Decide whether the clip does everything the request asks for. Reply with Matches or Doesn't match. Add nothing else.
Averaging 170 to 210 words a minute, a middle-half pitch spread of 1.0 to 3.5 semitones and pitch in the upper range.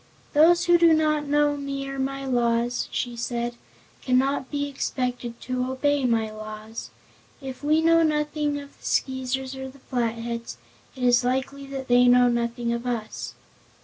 Doesn't match